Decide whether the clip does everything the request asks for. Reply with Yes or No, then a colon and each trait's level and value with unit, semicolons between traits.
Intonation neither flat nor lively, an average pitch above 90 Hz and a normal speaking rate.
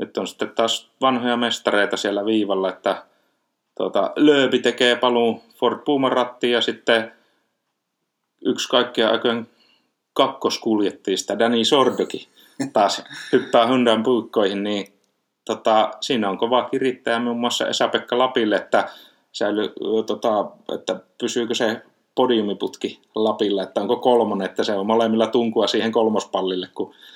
No: narrow, 1.7 semitones; low, 115 Hz; average, 125 wpm